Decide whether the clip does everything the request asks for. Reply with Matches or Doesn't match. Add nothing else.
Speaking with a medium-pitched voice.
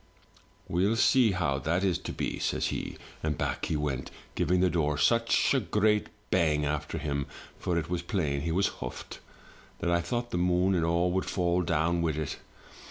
Doesn't match